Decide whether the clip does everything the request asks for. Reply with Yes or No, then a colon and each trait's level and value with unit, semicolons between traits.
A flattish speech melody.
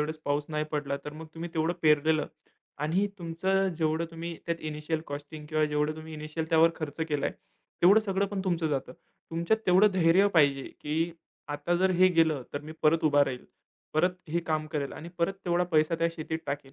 Yes: narrow, 2.1 semitones